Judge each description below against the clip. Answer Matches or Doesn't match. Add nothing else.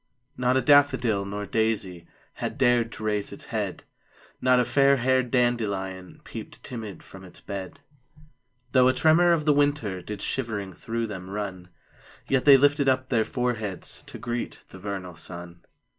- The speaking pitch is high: Doesn't match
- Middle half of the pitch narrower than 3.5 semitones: Doesn't match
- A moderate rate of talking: Matches